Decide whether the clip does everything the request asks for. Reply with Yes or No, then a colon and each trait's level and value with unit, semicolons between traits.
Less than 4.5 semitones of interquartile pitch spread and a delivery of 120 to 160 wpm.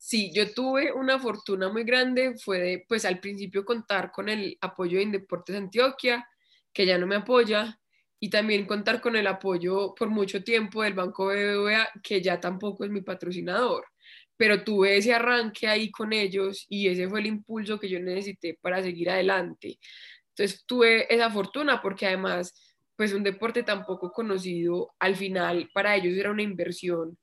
No: average, 2.9 semitones; average, 175 wpm